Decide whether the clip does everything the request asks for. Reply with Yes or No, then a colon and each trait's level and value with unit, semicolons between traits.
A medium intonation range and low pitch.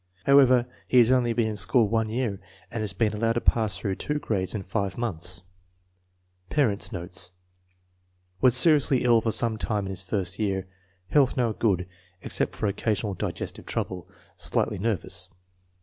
Yes: average, 3.8 semitones; low, 110 Hz